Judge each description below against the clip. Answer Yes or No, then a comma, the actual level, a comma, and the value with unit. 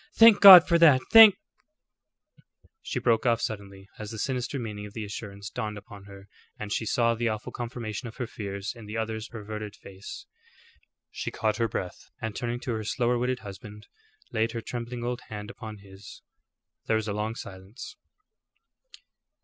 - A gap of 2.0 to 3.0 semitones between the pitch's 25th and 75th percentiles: Yes, average, 2.7 semitones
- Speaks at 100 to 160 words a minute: No, average, 175 wpm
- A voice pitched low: Yes, low, 110 Hz